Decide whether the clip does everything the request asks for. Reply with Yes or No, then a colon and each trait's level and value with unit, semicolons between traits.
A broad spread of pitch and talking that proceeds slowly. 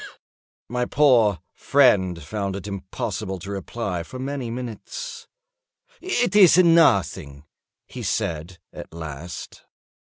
Yes: wide, 6.4 semitones; slow, 105 wpm